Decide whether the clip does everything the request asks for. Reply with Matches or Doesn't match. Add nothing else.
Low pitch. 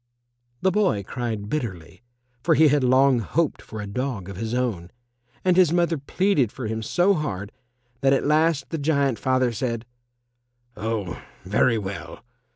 Matches